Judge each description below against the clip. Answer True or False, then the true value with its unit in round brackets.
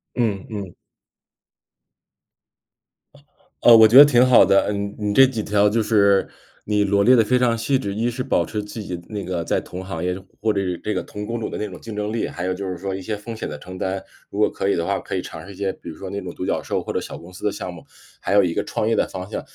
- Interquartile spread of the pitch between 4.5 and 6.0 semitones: False (3.0 semitones)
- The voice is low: True (100 Hz)